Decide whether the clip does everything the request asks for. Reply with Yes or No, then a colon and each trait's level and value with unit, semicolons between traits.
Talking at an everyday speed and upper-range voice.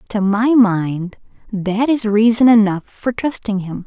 Yes: average, 155 wpm; high, 215 Hz